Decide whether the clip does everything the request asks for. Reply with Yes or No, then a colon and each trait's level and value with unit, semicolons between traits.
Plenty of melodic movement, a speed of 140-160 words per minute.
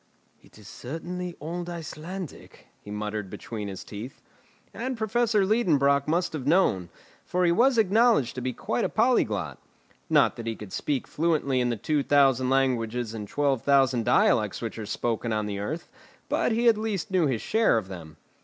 No: wide, 8.0 semitones; average, 180 wpm